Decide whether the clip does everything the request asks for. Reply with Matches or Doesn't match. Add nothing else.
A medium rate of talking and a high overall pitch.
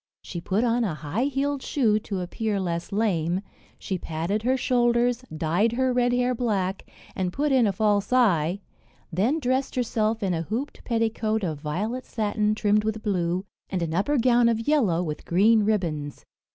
Matches